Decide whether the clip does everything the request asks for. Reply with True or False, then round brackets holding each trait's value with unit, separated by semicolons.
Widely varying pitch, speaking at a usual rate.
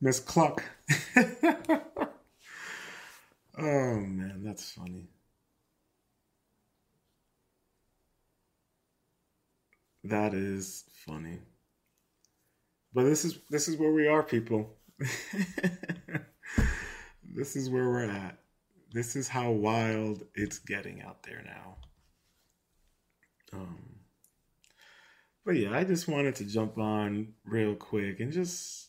False (7.5 semitones; 95 wpm)